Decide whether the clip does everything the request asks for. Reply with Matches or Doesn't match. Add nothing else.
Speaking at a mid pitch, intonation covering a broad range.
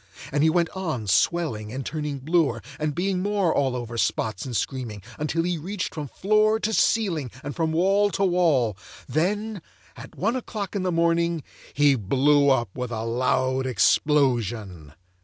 Matches